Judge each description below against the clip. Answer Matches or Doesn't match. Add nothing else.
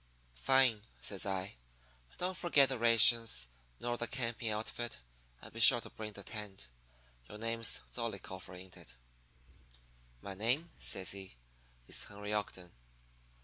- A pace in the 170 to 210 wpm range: Doesn't match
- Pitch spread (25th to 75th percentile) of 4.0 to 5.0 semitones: Doesn't match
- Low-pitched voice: Matches